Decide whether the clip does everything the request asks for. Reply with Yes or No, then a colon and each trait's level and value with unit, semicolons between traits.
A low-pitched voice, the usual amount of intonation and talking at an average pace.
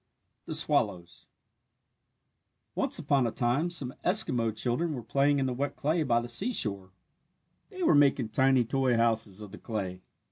Yes: low, 125 Hz; average, 4.2 semitones; average, 155 wpm